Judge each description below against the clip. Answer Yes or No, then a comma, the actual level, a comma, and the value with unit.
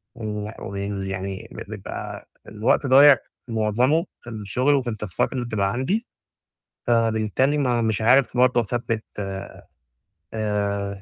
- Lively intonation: No, average, 3.5 semitones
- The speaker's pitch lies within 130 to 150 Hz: No, low, 115 Hz